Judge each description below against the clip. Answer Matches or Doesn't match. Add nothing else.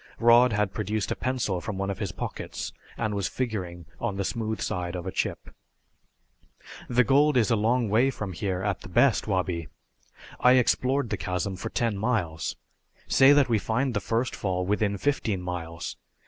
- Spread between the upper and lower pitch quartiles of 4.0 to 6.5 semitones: Matches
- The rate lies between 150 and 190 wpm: Matches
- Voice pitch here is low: Matches